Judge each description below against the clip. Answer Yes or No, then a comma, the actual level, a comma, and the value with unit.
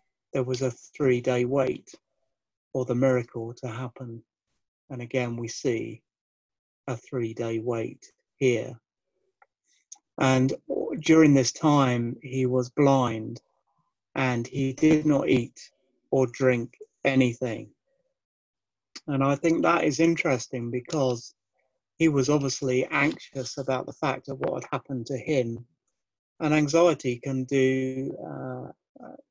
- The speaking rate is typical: No, slow, 125 wpm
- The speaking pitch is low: Yes, low, 130 Hz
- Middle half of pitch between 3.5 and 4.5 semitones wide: No, average, 3.0 semitones